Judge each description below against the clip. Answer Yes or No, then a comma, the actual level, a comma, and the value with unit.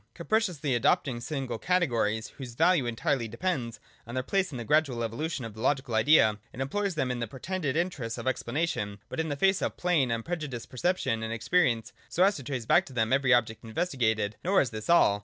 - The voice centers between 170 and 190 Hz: No, low, 130 Hz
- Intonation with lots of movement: Yes, wide, 6.2 semitones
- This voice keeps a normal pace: No, fast, 210 wpm